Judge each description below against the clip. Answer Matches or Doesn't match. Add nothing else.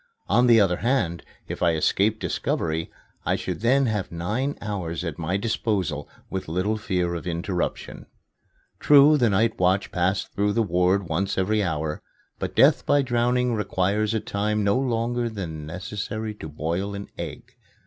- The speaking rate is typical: Matches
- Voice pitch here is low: Matches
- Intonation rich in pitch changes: Doesn't match